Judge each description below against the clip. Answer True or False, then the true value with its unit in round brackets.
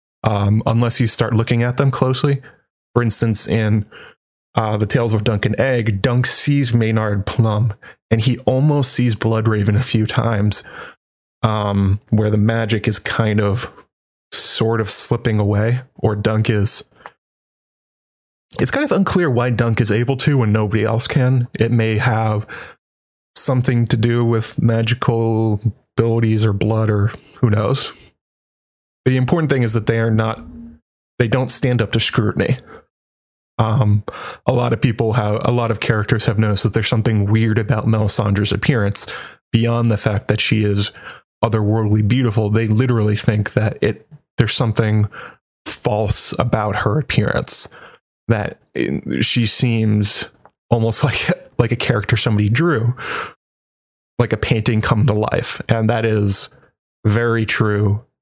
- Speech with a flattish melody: True (2.3 semitones)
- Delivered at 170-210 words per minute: False (150 wpm)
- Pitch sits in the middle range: False (115 Hz)